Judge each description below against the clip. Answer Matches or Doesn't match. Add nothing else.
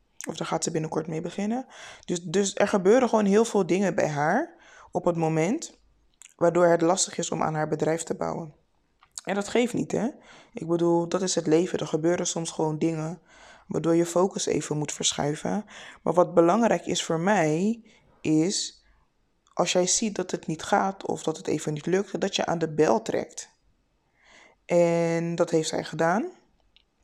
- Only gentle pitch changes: Doesn't match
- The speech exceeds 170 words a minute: Matches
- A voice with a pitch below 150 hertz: Doesn't match